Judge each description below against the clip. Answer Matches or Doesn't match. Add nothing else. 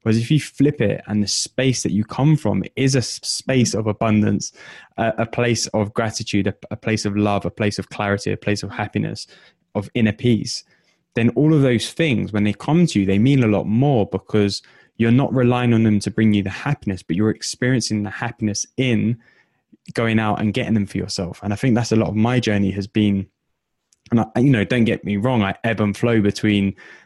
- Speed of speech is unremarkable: Doesn't match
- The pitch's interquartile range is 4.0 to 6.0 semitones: Doesn't match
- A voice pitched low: Matches